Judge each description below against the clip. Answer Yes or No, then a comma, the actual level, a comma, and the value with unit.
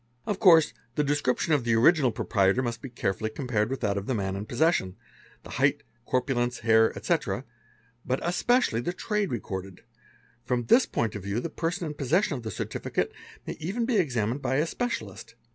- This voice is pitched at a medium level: No, low, 125 Hz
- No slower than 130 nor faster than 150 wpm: No, average, 190 wpm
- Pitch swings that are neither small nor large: No, wide, 6.5 semitones